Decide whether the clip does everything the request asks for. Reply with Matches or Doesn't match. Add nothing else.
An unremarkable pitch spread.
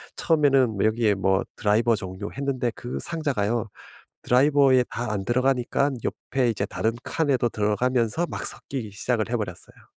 Matches